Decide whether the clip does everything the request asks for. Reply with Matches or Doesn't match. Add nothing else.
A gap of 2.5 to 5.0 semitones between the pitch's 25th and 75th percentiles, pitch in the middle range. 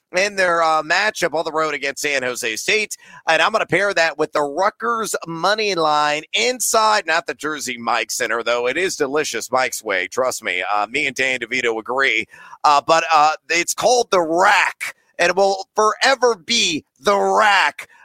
Doesn't match